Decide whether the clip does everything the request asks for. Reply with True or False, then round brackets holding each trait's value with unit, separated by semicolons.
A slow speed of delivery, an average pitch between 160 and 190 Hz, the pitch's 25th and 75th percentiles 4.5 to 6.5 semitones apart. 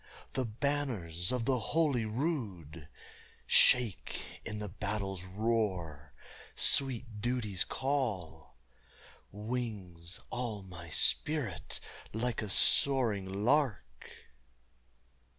False (85 wpm; 105 Hz; 5.4 semitones)